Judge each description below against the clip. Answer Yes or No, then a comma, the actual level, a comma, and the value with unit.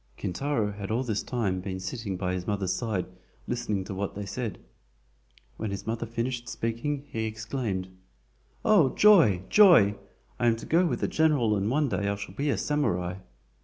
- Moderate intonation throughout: Yes, average, 4.7 semitones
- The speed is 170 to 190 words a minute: Yes, average, 180 wpm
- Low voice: Yes, low, 110 Hz